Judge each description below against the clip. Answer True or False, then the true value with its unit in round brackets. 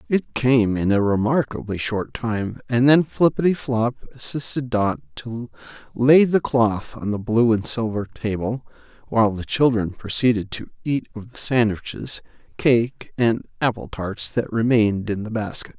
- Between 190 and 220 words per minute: False (150 wpm)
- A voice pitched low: True (115 Hz)